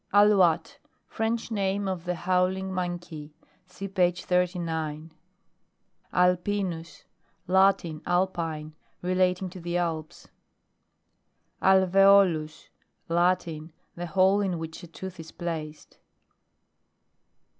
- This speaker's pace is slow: Yes, slow, 95 wpm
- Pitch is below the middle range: No, medium, 180 Hz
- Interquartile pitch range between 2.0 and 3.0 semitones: Yes, narrow, 2.5 semitones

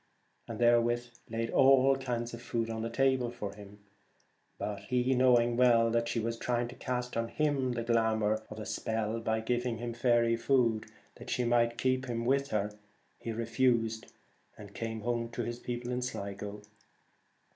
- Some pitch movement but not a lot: No, narrow, 1.4 semitones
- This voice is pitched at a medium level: No, low, 120 Hz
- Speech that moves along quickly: No, average, 155 wpm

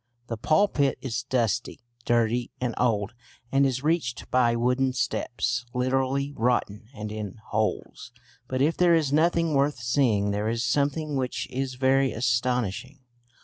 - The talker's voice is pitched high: No, low, 125 Hz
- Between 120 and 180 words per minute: Yes, average, 145 wpm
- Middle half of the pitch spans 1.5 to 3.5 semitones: Yes, average, 2.9 semitones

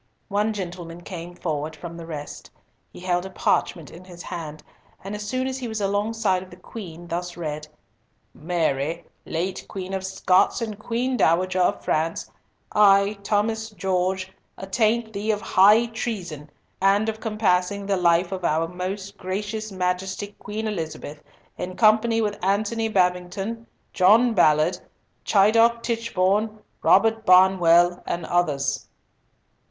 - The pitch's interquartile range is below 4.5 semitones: Yes, average, 3.5 semitones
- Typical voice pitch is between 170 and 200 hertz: Yes, high, 190 Hz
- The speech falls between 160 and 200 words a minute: No, average, 140 wpm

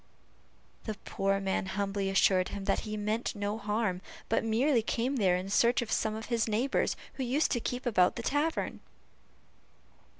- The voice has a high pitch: Yes, high, 215 Hz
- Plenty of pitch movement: No, average, 3.3 semitones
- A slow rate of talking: No, average, 170 wpm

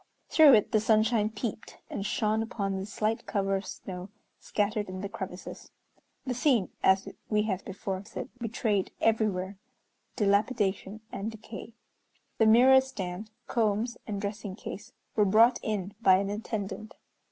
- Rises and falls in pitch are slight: Yes, narrow, 2.3 semitones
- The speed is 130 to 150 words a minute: Yes, average, 145 wpm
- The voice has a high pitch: Yes, high, 210 Hz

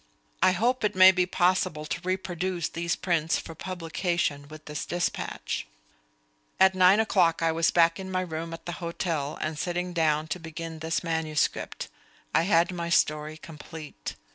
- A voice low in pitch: No, medium, 170 Hz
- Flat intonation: Yes, narrow, 2.2 semitones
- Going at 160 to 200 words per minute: Yes, average, 165 wpm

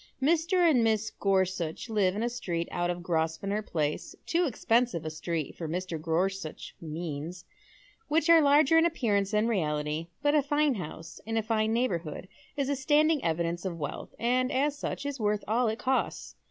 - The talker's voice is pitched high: Yes, high, 210 Hz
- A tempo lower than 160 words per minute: No, average, 180 wpm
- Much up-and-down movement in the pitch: Yes, wide, 7.8 semitones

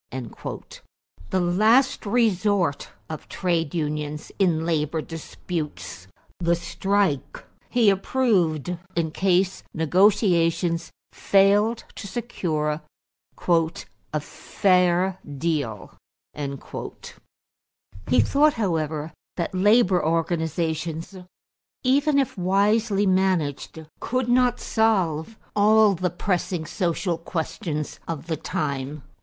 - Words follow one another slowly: Yes, slow, 90 wpm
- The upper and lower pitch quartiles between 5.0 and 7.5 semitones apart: No, average, 4.2 semitones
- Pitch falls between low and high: Yes, medium, 175 Hz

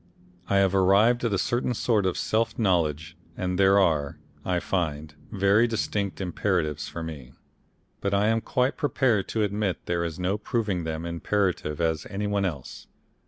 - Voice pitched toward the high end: No, very low, 95 Hz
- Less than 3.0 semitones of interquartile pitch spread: No, average, 3.8 semitones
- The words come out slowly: No, average, 165 wpm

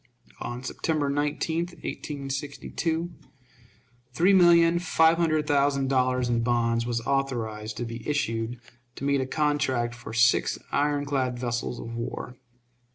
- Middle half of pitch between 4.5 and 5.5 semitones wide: No, average, 3.8 semitones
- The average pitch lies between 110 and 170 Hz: Yes, low, 135 Hz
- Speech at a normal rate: No, slow, 130 wpm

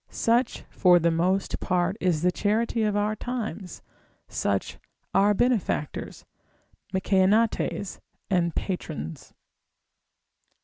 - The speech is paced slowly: Yes, slow, 95 wpm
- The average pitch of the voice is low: No, high, 195 Hz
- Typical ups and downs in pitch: Yes, average, 3.3 semitones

